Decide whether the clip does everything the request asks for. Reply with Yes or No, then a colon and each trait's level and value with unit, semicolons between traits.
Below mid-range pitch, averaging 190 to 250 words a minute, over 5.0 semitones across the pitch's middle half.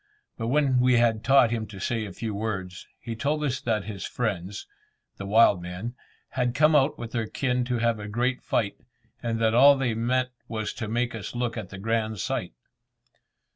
No: low, 115 Hz; average, 200 wpm; narrow, 2.6 semitones